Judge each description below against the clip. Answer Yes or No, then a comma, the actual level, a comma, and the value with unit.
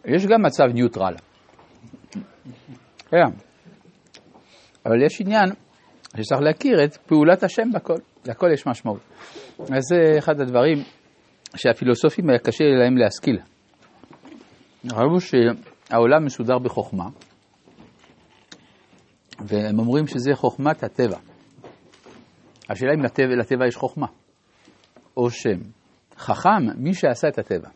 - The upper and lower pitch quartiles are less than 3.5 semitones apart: No, average, 4.5 semitones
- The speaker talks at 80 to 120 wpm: Yes, average, 105 wpm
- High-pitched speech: No, low, 135 Hz